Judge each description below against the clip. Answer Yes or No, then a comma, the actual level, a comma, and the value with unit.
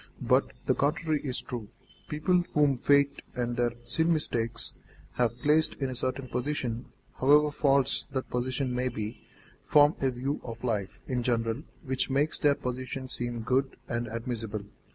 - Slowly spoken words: No, average, 155 wpm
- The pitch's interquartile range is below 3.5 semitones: Yes, average, 3.0 semitones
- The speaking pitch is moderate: No, low, 130 Hz